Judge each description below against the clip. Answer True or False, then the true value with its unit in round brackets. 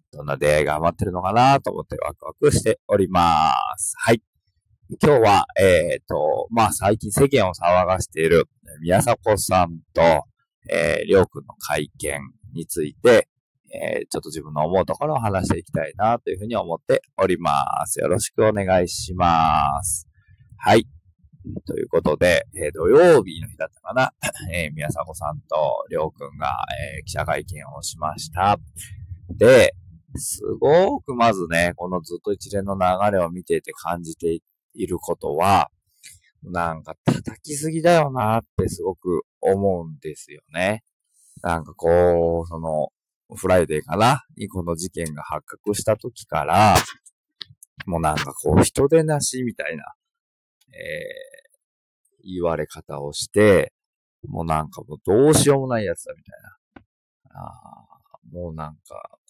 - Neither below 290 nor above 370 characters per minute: True (295 characters per minute)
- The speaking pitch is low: True (100 Hz)